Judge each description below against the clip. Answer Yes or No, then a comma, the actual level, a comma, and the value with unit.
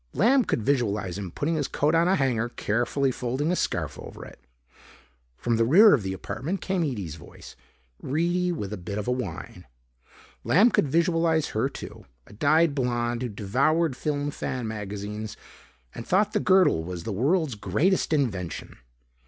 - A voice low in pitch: Yes, low, 130 Hz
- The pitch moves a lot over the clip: Yes, wide, 7.6 semitones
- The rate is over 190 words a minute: No, average, 170 wpm